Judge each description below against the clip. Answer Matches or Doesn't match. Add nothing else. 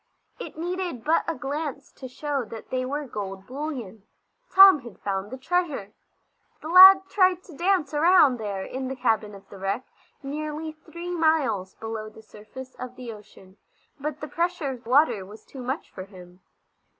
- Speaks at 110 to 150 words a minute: Doesn't match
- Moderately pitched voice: Doesn't match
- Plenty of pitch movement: Matches